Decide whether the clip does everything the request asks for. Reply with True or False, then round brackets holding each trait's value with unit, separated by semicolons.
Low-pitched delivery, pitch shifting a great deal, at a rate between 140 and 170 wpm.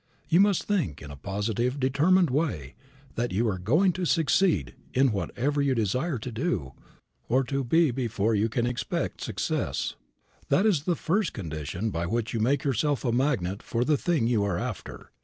False (125 Hz; 6.3 semitones; 180 wpm)